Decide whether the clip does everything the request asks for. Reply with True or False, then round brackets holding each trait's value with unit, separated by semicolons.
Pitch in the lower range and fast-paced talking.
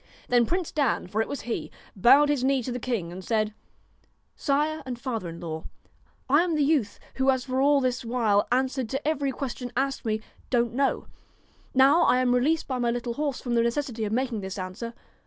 False (250 Hz; 215 wpm)